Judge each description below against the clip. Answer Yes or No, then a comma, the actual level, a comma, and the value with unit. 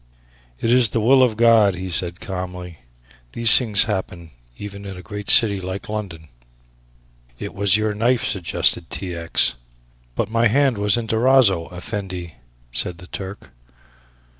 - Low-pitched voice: Yes, low, 100 Hz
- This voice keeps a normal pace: Yes, average, 150 wpm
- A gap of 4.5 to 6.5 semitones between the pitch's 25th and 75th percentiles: No, average, 3.8 semitones